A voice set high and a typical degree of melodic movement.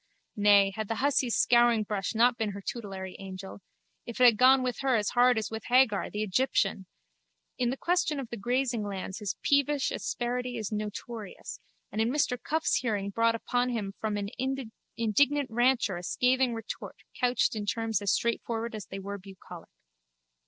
Yes: high, 230 Hz; average, 3.5 semitones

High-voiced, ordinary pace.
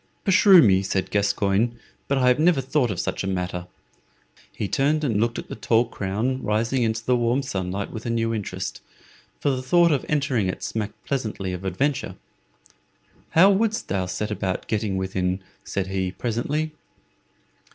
No: low, 115 Hz; average, 170 wpm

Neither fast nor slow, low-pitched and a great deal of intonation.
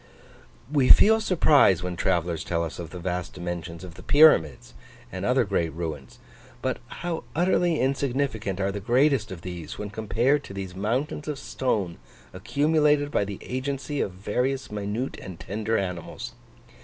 Yes: average, 155 wpm; low, 105 Hz; wide, 7.6 semitones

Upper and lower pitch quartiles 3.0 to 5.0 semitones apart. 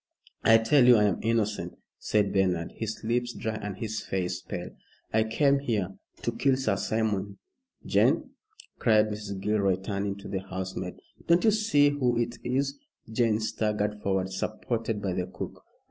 Yes: average, 3.3 semitones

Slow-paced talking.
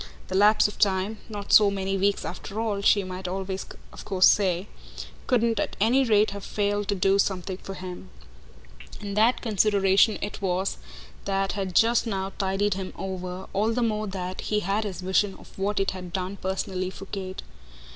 No: average, 185 wpm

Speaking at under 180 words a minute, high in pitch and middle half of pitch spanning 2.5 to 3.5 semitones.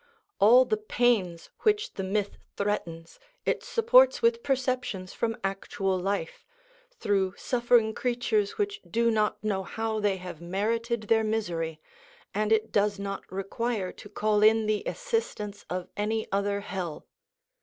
Yes: average, 140 wpm; high, 210 Hz; average, 3.2 semitones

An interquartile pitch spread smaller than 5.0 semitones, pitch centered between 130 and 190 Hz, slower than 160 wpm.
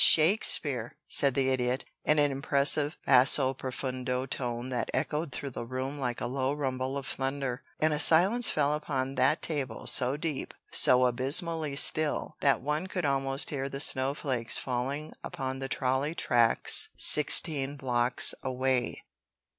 Yes: narrow, 2.4 semitones; low, 135 Hz; average, 145 wpm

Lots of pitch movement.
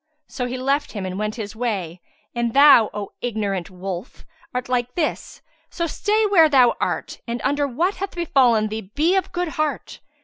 Yes: wide, 6.2 semitones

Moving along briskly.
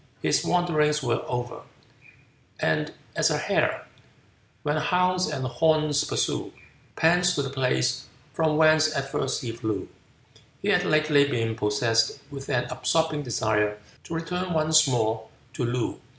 No: average, 140 wpm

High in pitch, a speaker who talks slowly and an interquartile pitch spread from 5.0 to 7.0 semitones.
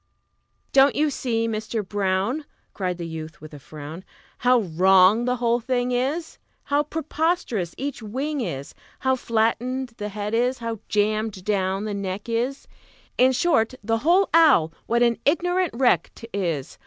No: high, 230 Hz; average, 155 wpm; average, 5.3 semitones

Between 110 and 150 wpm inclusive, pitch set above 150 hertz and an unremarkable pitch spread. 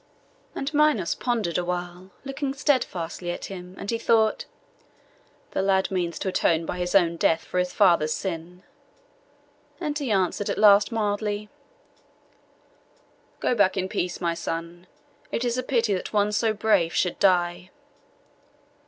Yes: average, 145 wpm; high, 190 Hz; average, 3.8 semitones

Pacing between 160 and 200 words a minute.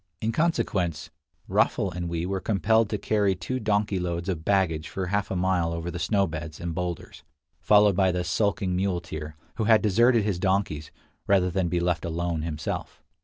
Yes: average, 180 wpm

